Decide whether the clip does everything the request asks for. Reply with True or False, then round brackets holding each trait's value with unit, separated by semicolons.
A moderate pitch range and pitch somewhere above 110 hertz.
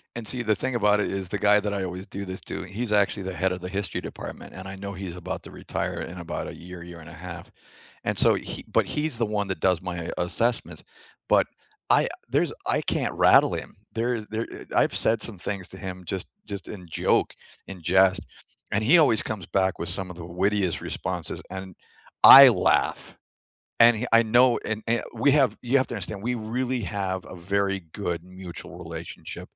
False (3.1 semitones; 95 Hz)